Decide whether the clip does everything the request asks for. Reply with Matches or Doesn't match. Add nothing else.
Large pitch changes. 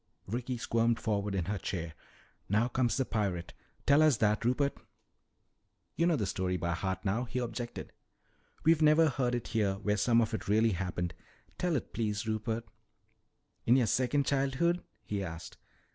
Doesn't match